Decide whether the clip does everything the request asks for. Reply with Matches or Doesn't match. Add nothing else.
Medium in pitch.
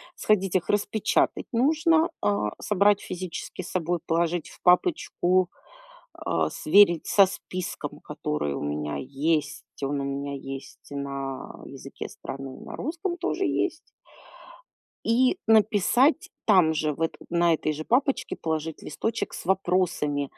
Matches